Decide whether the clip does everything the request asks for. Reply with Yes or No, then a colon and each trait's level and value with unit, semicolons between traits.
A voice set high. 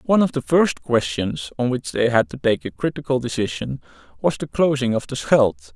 No: low, 125 Hz